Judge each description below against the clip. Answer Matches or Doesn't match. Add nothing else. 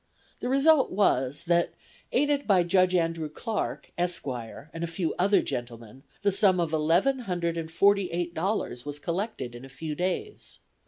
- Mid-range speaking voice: Matches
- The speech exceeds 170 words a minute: Doesn't match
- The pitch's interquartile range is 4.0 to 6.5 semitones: Matches